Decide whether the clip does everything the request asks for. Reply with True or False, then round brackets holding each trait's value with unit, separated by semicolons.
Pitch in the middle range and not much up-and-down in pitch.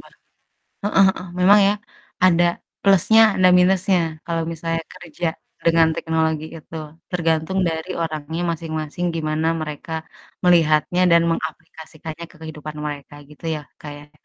True (165 Hz; 2.2 semitones)